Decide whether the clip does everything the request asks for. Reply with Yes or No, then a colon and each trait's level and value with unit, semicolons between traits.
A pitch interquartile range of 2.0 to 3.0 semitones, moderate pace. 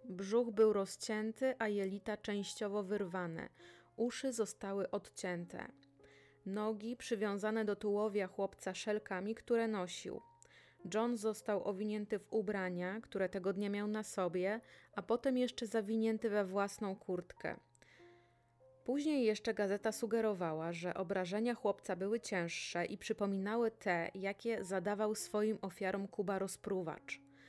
Yes: average, 2.7 semitones; average, 120 wpm